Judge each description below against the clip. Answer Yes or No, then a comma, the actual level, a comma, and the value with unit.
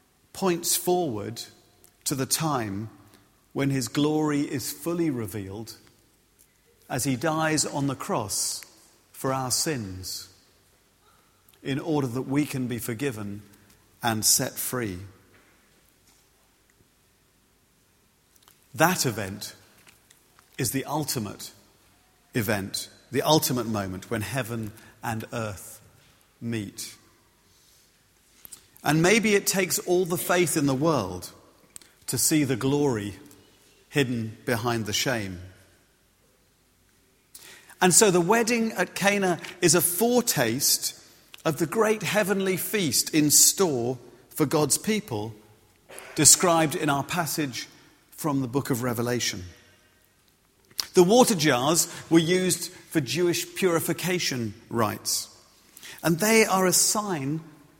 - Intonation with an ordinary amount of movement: No, wide, 7.4 semitones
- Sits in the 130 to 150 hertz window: Yes, medium, 140 Hz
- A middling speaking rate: No, slow, 110 wpm